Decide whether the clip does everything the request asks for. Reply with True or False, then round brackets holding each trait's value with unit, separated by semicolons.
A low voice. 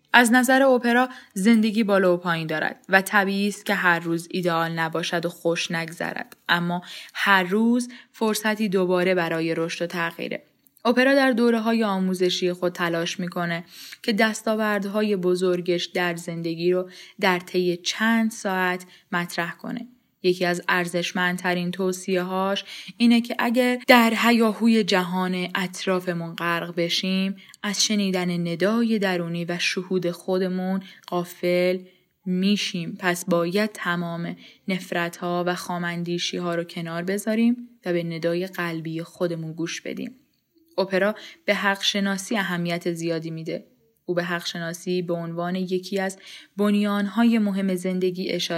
False (185 Hz)